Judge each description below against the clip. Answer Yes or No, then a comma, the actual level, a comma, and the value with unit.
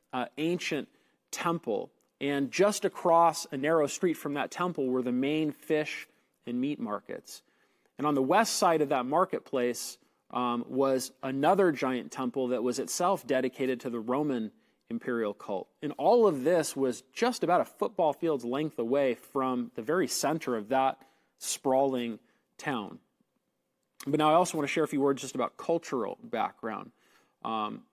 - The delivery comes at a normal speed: Yes, average, 165 wpm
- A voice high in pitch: No, medium, 140 Hz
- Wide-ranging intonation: No, average, 3.7 semitones